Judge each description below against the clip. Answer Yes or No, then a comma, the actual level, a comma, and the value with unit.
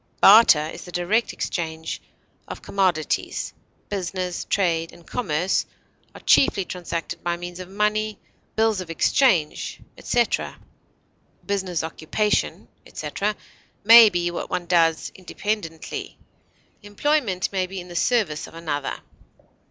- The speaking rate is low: Yes, slow, 120 wpm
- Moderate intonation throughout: Yes, average, 3.8 semitones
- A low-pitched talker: No, medium, 180 Hz